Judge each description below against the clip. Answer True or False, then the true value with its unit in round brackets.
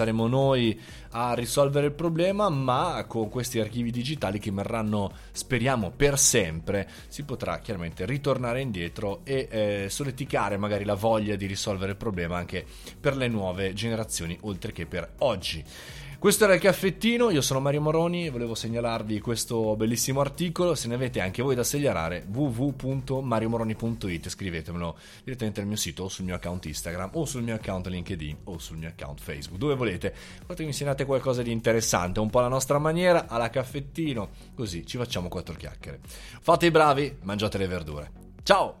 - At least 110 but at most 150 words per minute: False (170 wpm)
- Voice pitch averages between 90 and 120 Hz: True (115 Hz)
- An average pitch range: False (6.4 semitones)